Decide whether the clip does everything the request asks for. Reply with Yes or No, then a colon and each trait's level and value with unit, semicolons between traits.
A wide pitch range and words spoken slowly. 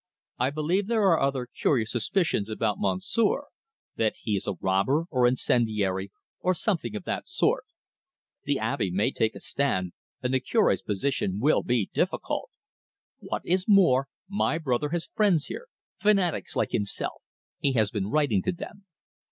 No: wide, 8.7 semitones; average, 160 wpm